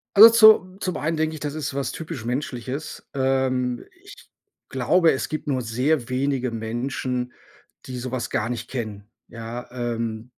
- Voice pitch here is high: No, low, 130 Hz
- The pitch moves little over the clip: No, average, 3.7 semitones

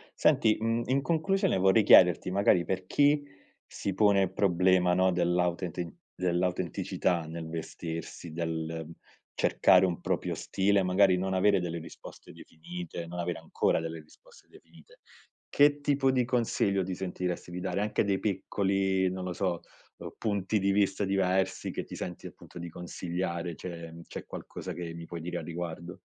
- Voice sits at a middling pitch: No, very low, 90 Hz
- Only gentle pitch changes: Yes, narrow, 2.3 semitones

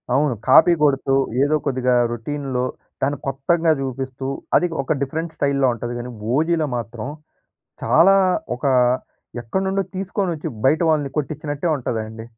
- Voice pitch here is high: No, medium, 140 Hz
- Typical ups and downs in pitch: Yes, average, 3.8 semitones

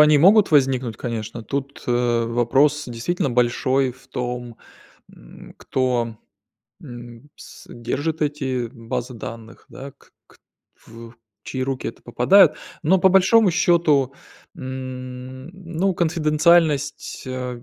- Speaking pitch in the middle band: No, low, 130 Hz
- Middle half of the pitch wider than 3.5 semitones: Yes, average, 4.0 semitones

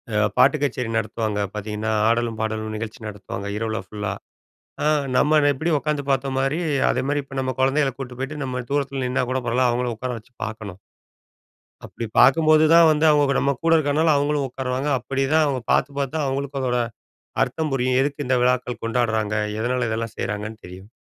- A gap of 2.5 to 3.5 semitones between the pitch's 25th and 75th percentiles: No, average, 4.0 semitones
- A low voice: Yes, low, 130 Hz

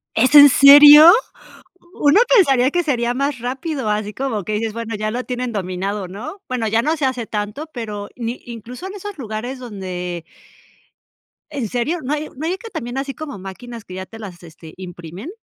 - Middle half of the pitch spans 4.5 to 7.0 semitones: Yes, average, 5.2 semitones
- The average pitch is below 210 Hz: No, high, 240 Hz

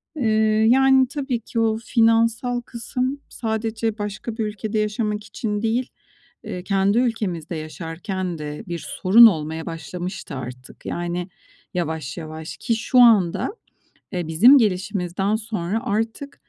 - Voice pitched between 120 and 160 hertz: No, high, 210 Hz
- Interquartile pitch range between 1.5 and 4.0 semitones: No, average, 4.7 semitones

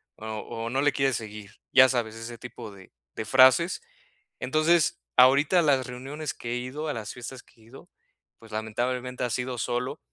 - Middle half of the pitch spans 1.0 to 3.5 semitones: Yes, average, 2.8 semitones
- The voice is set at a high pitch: No, low, 125 Hz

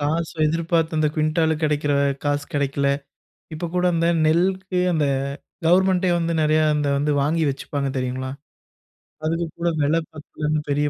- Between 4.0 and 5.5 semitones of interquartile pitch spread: No, narrow, 2.4 semitones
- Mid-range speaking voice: Yes, medium, 155 Hz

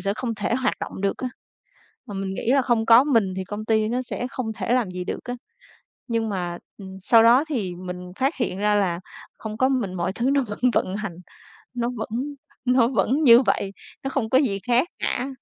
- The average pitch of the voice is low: No, high, 225 Hz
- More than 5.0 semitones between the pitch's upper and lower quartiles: No, average, 4.3 semitones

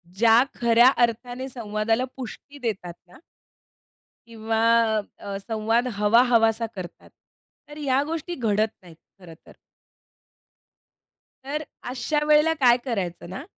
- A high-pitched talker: Yes, high, 230 Hz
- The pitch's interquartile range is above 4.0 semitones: No, average, 3.3 semitones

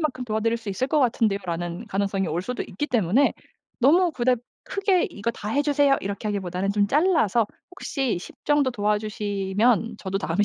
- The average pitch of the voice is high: Yes, high, 220 Hz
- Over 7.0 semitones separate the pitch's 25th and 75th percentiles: No, average, 5.3 semitones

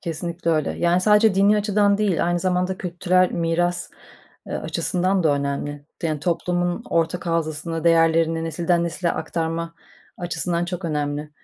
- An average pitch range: No, narrow, 1.8 semitones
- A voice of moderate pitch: Yes, medium, 170 Hz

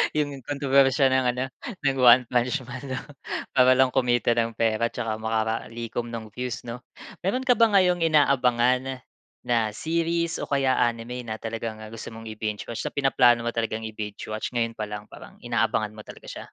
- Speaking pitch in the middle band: No, low, 120 Hz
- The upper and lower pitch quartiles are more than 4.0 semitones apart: No, average, 2.9 semitones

